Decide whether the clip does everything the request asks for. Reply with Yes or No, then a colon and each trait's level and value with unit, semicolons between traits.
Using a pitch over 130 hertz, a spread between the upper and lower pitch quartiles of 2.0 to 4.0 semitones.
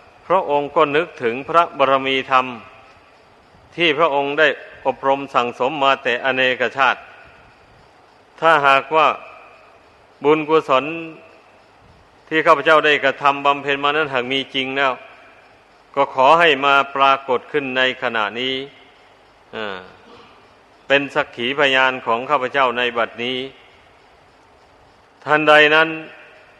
Yes: medium, 140 Hz; narrow, 2.6 semitones